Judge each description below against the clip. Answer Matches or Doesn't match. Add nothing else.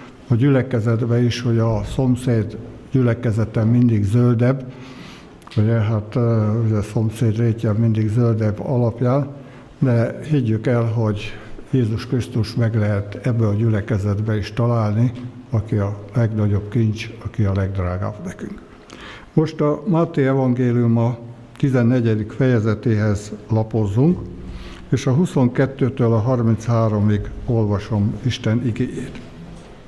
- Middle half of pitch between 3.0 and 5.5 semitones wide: Doesn't match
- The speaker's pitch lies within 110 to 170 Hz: Matches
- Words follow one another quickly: Doesn't match